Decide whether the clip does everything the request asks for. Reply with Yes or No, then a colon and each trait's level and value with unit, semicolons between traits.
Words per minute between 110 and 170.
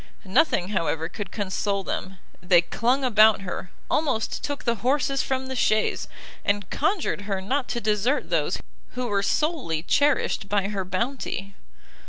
Yes: average, 150 wpm